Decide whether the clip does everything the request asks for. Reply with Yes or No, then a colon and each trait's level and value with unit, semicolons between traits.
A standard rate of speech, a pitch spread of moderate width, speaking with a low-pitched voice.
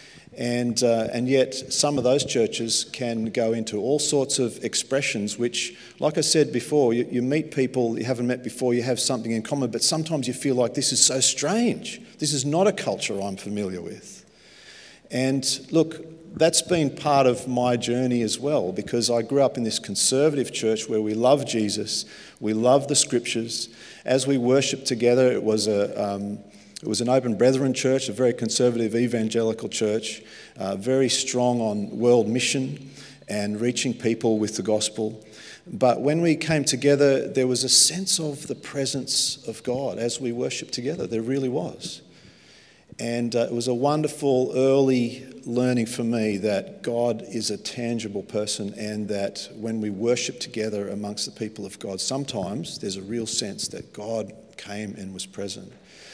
Yes: average, 175 wpm; average, 3.3 semitones; low, 120 Hz